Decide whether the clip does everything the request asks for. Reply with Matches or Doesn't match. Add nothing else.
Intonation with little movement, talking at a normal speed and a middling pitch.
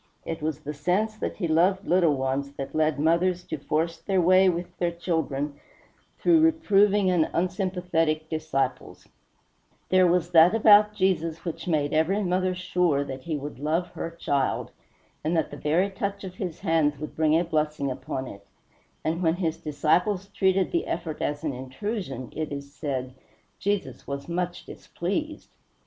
Doesn't match